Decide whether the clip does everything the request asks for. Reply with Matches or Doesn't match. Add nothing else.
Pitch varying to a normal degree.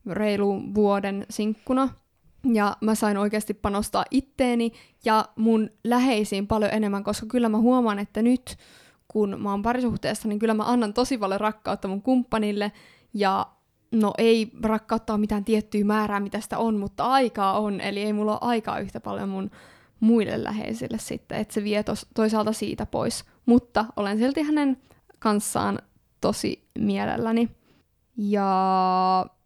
Doesn't match